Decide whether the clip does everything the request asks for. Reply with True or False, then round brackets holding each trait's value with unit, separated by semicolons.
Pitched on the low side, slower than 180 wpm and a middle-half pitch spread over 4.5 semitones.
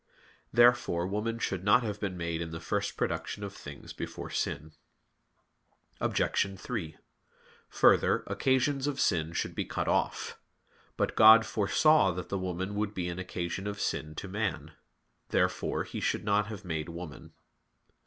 False (100 Hz; 155 wpm; 4.0 semitones)